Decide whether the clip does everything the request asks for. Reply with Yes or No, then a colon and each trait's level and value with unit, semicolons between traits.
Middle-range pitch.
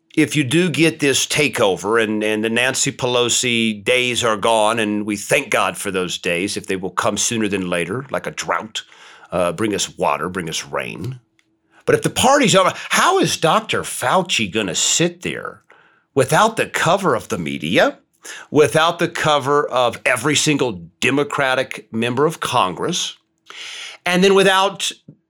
No: low, 130 Hz